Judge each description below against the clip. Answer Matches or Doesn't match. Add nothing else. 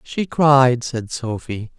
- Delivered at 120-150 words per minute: Matches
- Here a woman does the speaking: Doesn't match